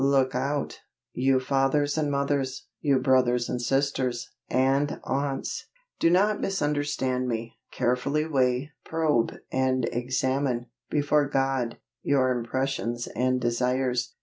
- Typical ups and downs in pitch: No, narrow, 2.1 semitones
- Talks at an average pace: No, slow, 115 wpm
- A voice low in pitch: Yes, low, 130 Hz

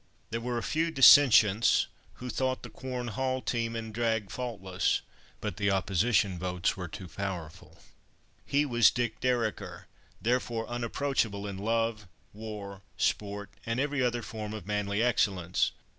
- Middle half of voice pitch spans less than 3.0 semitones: No, average, 3.4 semitones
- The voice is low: Yes, low, 110 Hz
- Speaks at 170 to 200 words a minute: No, average, 145 wpm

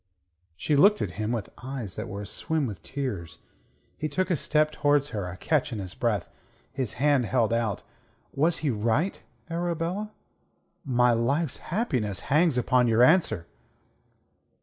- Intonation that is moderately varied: No, wide, 5.7 semitones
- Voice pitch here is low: Yes, low, 130 Hz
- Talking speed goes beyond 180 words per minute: No, average, 150 wpm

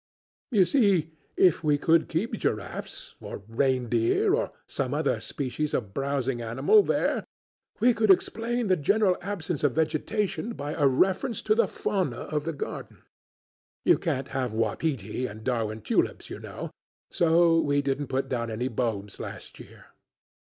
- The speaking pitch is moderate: Yes, medium, 145 Hz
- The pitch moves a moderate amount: No, wide, 6.8 semitones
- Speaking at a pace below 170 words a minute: Yes, average, 155 wpm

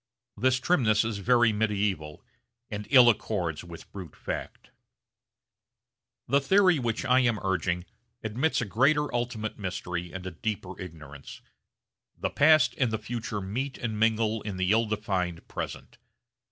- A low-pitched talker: Yes, low, 110 Hz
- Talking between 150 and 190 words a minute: No, average, 140 wpm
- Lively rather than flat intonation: No, average, 4.6 semitones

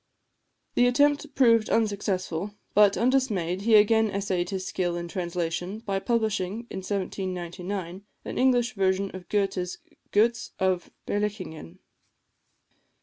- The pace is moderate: No, slow, 115 wpm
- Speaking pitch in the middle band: No, high, 200 Hz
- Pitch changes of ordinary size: Yes, average, 3.3 semitones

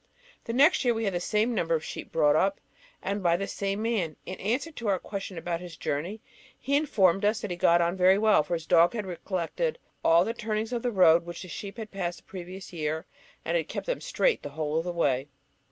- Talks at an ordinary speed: No, fast, 245 wpm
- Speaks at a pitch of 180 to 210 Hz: Yes, high, 190 Hz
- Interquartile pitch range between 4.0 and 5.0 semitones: Yes, average, 4.4 semitones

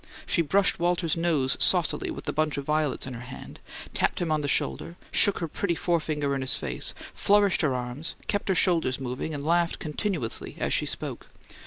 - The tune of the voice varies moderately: Yes, average, 3.7 semitones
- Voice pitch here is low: No, medium, 155 Hz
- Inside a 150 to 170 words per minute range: No, average, 195 wpm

